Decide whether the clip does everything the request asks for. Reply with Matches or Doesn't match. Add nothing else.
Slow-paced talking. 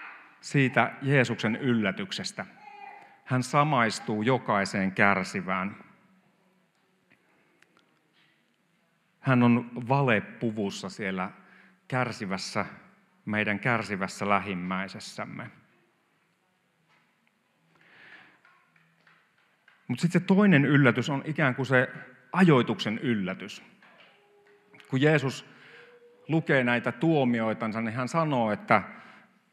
Matches